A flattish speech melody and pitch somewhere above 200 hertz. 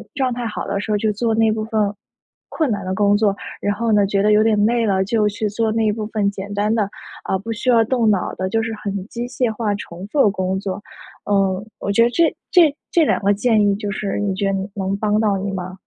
Yes: narrow, 2.1 semitones; high, 210 Hz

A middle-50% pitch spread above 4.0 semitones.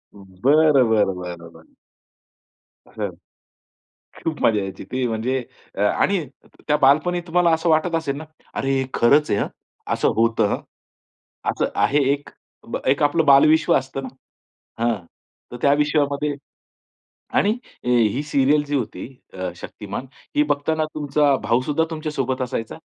Yes: average, 4.4 semitones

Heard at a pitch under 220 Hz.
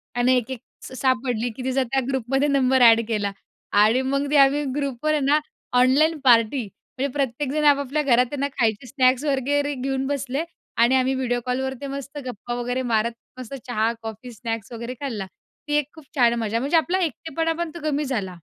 No: very high, 260 Hz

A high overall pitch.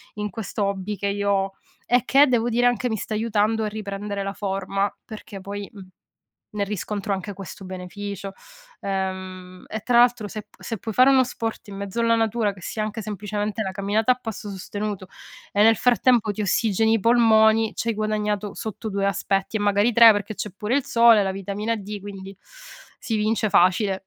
Yes: high, 210 Hz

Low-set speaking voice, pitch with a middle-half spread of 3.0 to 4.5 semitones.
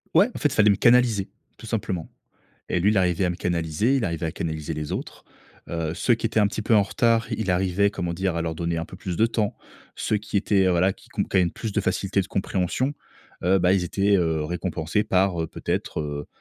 Yes: very low, 95 Hz; average, 3.8 semitones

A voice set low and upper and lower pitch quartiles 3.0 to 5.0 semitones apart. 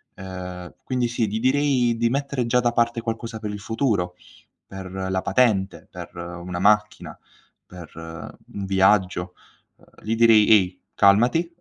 Yes: low, 105 Hz; average, 4.2 semitones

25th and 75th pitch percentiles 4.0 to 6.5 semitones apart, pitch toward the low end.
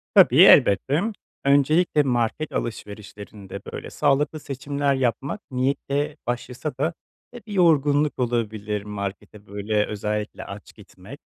Yes: wide, 5.5 semitones; low, 130 Hz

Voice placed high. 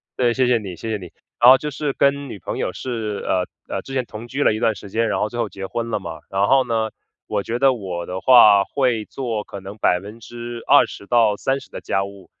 No: low, 115 Hz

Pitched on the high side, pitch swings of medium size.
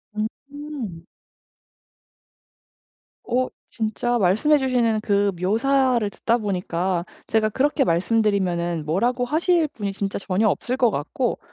Yes: high, 220 Hz; average, 4.8 semitones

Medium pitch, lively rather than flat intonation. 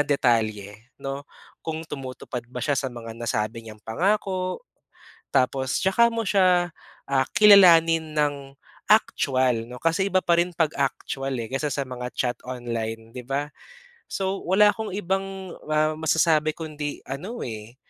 Yes: medium, 145 Hz; wide, 6.3 semitones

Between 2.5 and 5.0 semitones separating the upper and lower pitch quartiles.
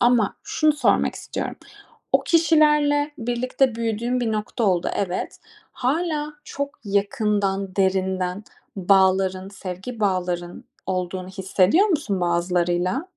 No: wide, 5.4 semitones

